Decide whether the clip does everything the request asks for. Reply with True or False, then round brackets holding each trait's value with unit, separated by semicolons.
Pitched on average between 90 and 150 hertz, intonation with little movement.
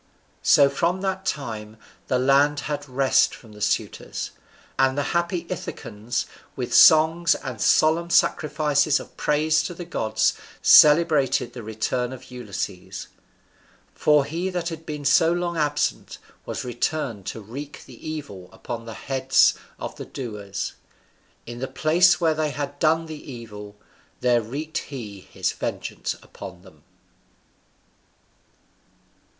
False (140 Hz; 4.9 semitones)